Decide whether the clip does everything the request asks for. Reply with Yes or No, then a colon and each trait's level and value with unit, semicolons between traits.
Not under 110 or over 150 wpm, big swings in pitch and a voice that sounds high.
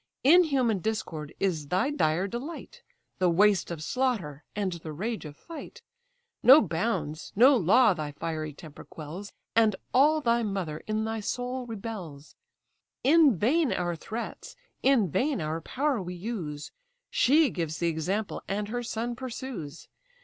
Yes: average, 145 wpm; wide, 7.1 semitones; high, 210 Hz